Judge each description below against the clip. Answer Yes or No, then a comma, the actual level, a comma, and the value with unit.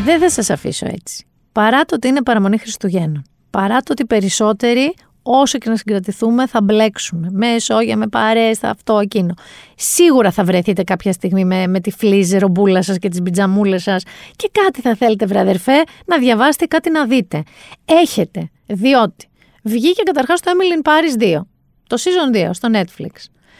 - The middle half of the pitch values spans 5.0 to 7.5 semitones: Yes, wide, 5.5 semitones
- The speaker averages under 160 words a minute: No, fast, 170 wpm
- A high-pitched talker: Yes, high, 220 Hz